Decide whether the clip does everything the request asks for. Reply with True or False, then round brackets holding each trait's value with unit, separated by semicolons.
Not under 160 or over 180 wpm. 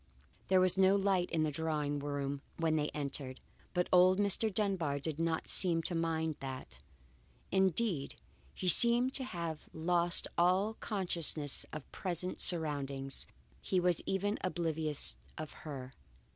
False (140 wpm)